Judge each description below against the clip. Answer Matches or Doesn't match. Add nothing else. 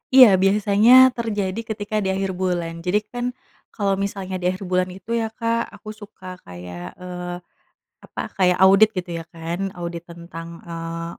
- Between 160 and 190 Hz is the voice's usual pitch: Matches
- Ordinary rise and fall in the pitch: Matches